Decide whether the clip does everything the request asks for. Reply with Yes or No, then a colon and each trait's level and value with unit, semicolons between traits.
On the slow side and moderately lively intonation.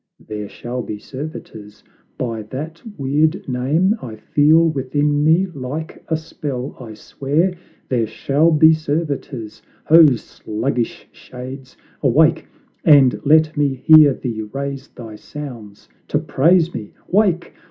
Yes: slow, 125 wpm; average, 4.2 semitones